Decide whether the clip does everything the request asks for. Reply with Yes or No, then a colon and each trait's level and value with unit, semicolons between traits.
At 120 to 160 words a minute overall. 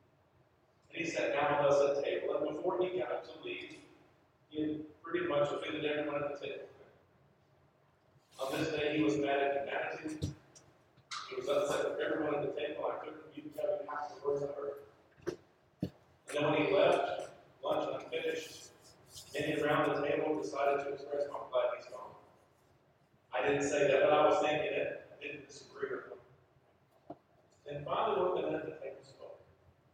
No: average, 175 wpm